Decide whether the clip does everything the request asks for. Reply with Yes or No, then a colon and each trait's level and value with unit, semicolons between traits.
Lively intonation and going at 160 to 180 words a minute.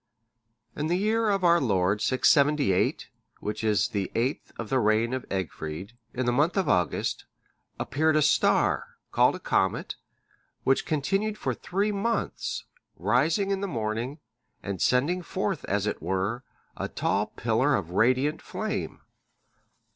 No: wide, 8.4 semitones; average, 145 wpm